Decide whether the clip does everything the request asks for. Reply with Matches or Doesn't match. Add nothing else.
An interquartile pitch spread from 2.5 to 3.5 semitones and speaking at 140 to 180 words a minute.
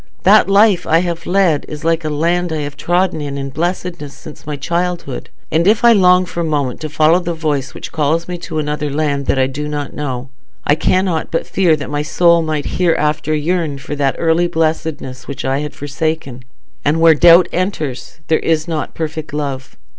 Doesn't match